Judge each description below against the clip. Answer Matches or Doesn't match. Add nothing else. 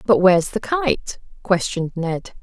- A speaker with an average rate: Matches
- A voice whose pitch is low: Doesn't match